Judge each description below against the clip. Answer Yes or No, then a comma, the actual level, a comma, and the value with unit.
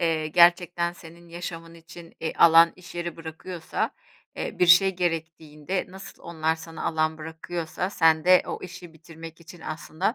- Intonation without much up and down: Yes, narrow, 1.5 semitones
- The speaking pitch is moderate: Yes, medium, 165 Hz